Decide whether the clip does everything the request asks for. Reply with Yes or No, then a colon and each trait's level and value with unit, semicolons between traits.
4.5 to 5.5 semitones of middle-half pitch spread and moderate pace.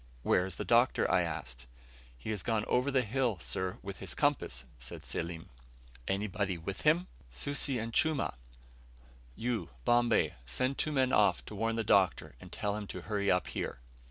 Yes: average, 5.1 semitones; average, 175 wpm